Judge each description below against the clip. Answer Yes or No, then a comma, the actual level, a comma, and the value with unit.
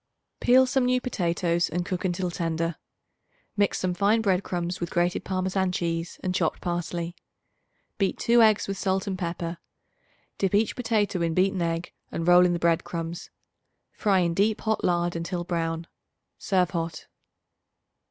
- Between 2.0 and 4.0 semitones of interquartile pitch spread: Yes, narrow, 2.5 semitones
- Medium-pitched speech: Yes, medium, 180 Hz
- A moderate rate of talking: Yes, average, 160 wpm